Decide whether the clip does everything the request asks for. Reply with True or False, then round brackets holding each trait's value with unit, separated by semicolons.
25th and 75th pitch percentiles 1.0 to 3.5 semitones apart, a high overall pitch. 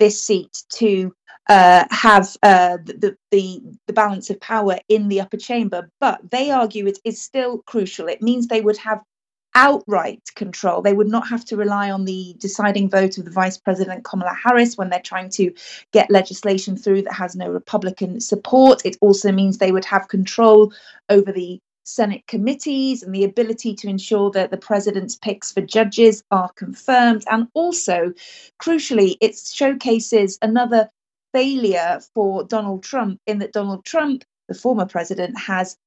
True (2.8 semitones; 205 Hz)